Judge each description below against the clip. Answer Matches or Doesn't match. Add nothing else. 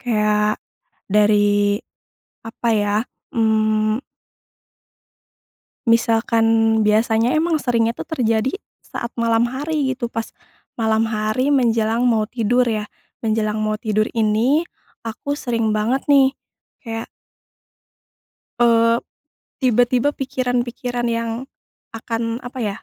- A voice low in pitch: Doesn't match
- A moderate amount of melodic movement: Doesn't match